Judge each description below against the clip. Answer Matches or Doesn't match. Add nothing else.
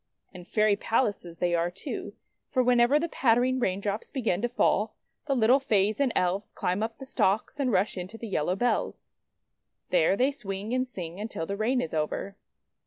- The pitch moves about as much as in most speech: Matches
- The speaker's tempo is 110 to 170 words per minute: Doesn't match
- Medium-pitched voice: Doesn't match